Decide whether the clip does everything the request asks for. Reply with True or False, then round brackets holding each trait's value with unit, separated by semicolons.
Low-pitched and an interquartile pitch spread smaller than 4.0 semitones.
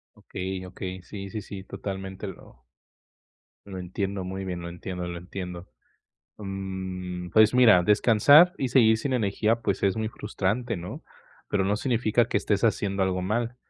True (95 Hz; 2.9 semitones)